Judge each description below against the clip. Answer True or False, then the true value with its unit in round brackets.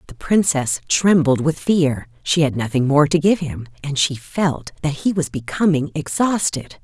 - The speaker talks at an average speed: True (175 wpm)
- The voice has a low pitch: False (150 Hz)